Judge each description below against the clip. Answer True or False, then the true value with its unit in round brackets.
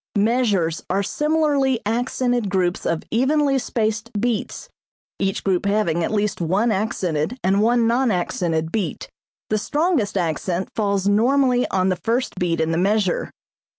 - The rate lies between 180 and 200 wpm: False (145 wpm)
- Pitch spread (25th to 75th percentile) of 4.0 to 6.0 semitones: True (4.9 semitones)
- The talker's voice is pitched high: True (210 Hz)